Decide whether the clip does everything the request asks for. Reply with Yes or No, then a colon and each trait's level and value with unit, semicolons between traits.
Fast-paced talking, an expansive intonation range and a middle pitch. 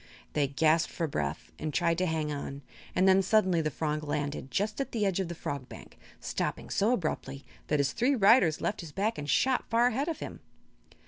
Yes: fast, 210 wpm; wide, 5.9 semitones; medium, 170 Hz